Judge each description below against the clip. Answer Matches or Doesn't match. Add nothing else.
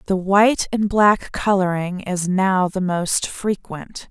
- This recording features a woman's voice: Matches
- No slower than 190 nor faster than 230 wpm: Doesn't match